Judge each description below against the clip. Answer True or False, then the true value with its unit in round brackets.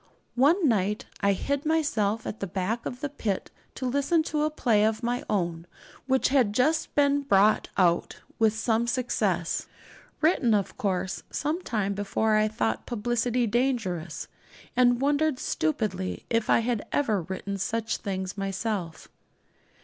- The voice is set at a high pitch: True (225 Hz)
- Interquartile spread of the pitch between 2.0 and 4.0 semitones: False (4.8 semitones)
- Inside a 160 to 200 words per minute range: False (150 wpm)